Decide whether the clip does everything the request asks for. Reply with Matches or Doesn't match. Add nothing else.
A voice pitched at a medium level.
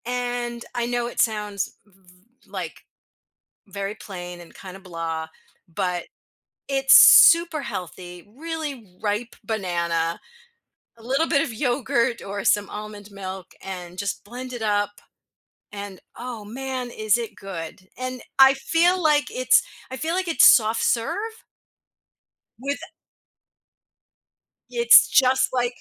Doesn't match